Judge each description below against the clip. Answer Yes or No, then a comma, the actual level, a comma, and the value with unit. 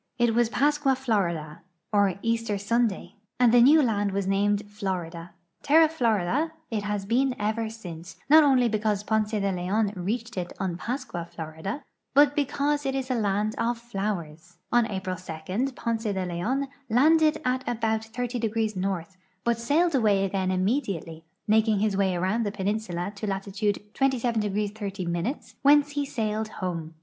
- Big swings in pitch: No, average, 4.2 semitones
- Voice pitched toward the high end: Yes, high, 215 Hz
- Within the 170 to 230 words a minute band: No, average, 155 wpm